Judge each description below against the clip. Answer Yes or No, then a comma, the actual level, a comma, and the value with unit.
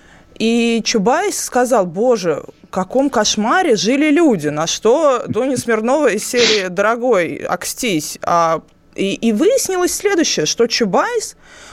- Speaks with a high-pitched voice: Yes, high, 235 Hz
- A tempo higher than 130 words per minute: No, average, 125 wpm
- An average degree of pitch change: No, wide, 6.0 semitones